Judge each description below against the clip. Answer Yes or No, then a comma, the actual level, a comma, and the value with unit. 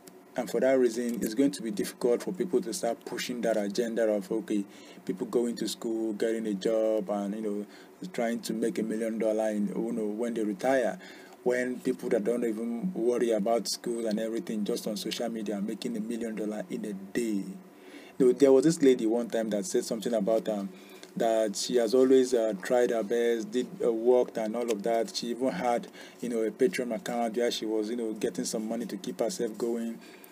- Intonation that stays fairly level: Yes, narrow, 1.8 semitones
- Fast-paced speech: Yes, fast, 215 wpm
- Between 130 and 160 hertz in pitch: No, low, 115 Hz